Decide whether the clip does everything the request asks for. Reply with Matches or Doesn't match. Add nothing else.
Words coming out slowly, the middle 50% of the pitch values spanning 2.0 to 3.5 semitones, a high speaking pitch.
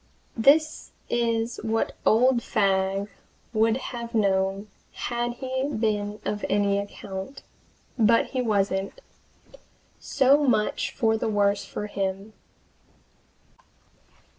Matches